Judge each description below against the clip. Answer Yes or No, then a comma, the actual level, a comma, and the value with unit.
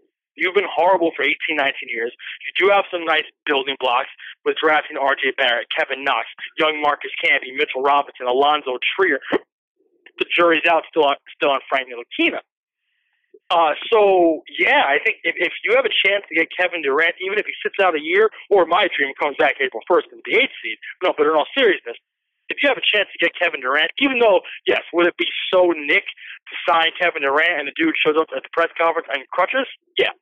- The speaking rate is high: Yes, fast, 210 wpm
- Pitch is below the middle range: No, high, 205 Hz